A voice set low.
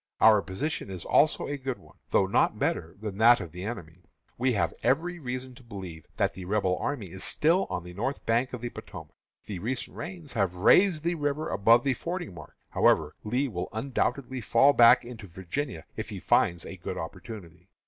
Yes: low, 115 Hz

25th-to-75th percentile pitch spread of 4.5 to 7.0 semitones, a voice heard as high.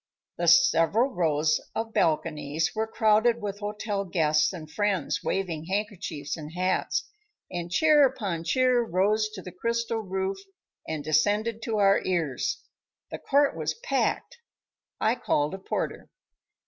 Yes: average, 5.2 semitones; high, 195 Hz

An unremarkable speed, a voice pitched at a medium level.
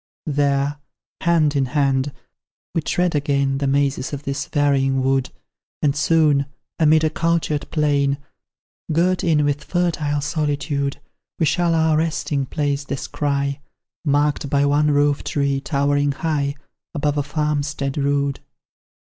No: slow, 130 wpm; medium, 145 Hz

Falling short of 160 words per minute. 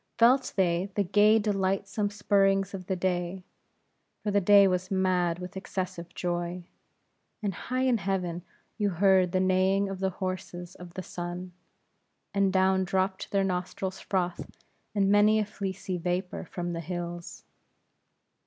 Yes: average, 145 wpm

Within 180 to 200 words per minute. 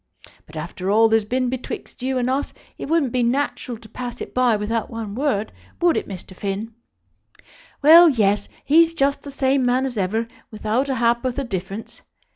Yes: average, 185 wpm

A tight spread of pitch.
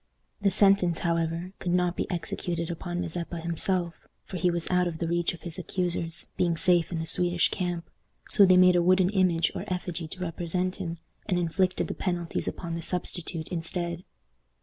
Yes: narrow, 1.4 semitones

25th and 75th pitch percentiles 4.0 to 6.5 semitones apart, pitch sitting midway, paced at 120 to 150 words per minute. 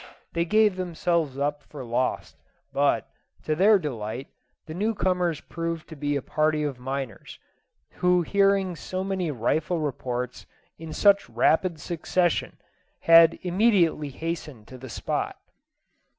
Yes: average, 4.5 semitones; medium, 160 Hz; slow, 135 wpm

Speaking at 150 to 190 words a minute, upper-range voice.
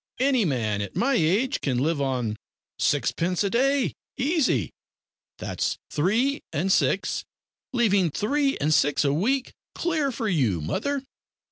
No: slow, 135 wpm; high, 195 Hz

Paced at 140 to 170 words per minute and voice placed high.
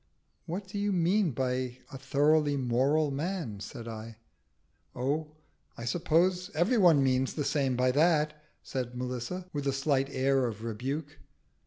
No: average, 150 wpm; medium, 140 Hz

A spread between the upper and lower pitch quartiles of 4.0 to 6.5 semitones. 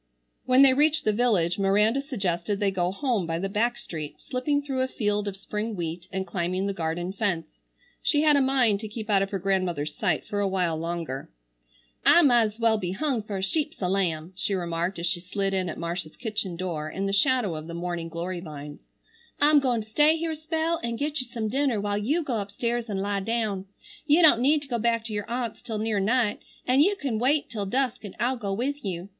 Yes: wide, 5.5 semitones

